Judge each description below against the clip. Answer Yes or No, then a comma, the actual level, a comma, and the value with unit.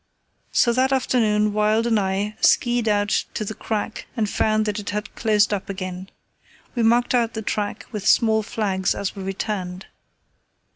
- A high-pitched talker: Yes, high, 210 Hz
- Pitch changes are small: Yes, narrow, 1.9 semitones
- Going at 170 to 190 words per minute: Yes, average, 175 wpm